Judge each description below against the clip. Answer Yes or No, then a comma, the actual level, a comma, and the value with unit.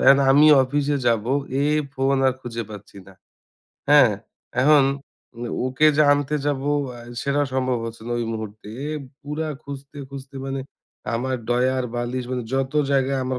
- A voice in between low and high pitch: No, low, 130 Hz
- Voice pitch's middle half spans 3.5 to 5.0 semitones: No, narrow, 2.5 semitones